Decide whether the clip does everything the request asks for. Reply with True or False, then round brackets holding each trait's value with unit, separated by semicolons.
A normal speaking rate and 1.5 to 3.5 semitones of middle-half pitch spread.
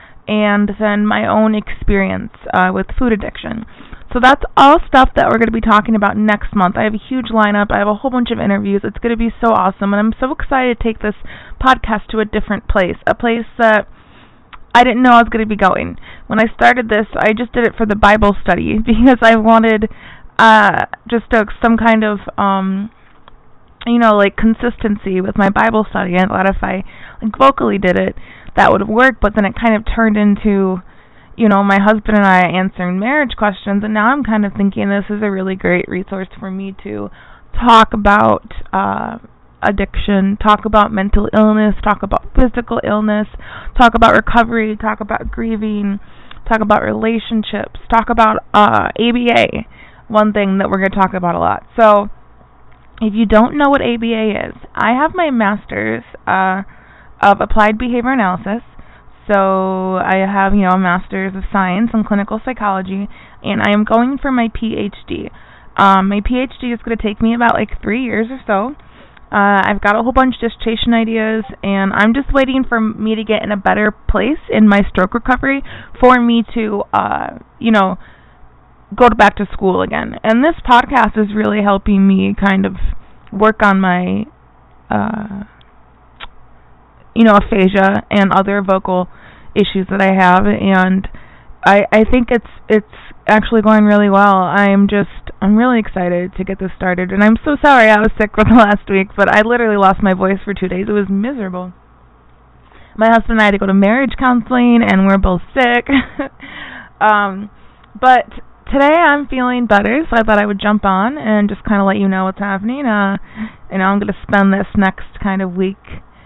True (190 wpm; 2.7 semitones)